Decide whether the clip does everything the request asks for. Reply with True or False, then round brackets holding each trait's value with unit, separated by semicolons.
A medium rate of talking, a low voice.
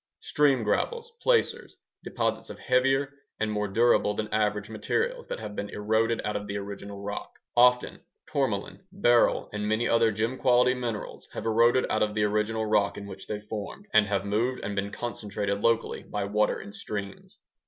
True (175 wpm; 110 Hz)